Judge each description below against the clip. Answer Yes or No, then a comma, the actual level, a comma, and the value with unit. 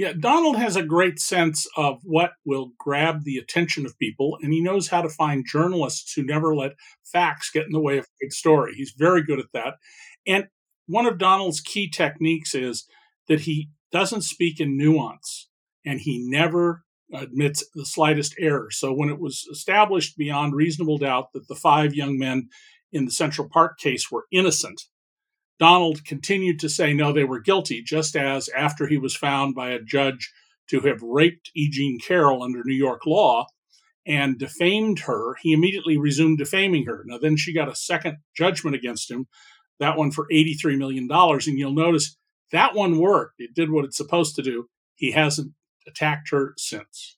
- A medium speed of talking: Yes, average, 185 wpm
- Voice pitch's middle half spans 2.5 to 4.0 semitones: Yes, average, 3.4 semitones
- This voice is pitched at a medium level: Yes, medium, 155 Hz